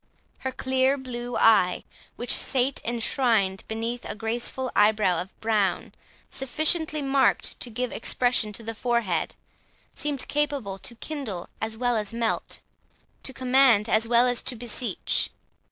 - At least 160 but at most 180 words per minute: No, slow, 135 wpm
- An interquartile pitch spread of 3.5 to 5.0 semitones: No, average, 3.1 semitones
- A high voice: Yes, high, 240 Hz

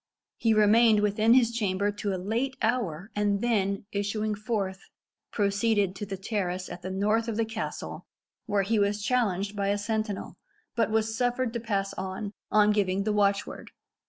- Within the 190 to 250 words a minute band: No, average, 175 wpm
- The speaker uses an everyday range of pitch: No, narrow, 2.0 semitones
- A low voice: No, high, 210 Hz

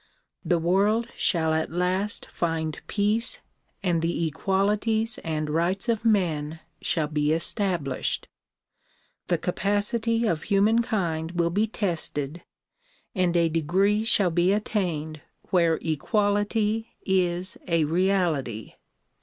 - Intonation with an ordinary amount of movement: Yes, average, 4.2 semitones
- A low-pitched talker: No, medium, 180 Hz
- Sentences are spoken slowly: Yes, slow, 110 wpm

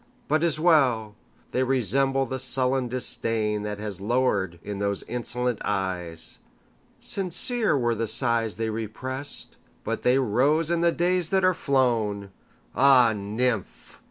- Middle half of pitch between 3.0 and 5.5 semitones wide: Yes, average, 4.4 semitones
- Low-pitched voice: Yes, low, 125 Hz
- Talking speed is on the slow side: Yes, slow, 120 wpm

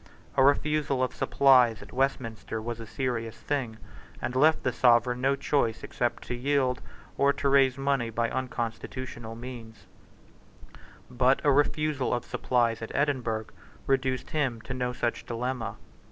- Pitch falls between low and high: No, low, 125 Hz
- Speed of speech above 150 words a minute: No, average, 145 wpm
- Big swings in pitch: No, narrow, 2.6 semitones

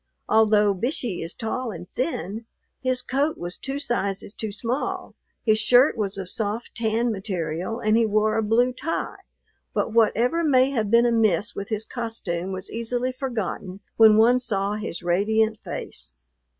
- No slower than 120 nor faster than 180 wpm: Yes, average, 160 wpm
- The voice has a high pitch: Yes, high, 220 Hz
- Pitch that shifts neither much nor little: Yes, average, 3.3 semitones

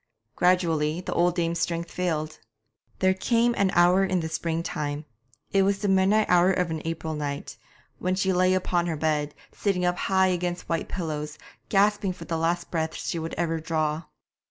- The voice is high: No, medium, 175 Hz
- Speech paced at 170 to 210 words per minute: Yes, average, 185 wpm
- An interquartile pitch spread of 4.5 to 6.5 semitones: No, narrow, 2.6 semitones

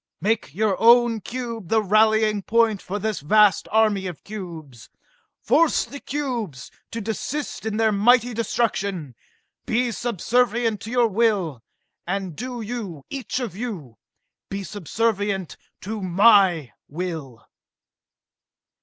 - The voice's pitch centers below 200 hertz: No, high, 215 Hz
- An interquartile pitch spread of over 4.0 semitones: No, average, 3.7 semitones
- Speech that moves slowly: Yes, slow, 120 wpm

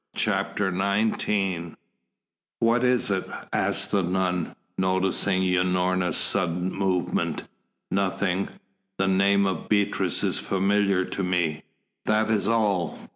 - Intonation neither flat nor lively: No, narrow, 1.7 semitones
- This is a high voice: No, very low, 95 Hz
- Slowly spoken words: Yes, slow, 110 wpm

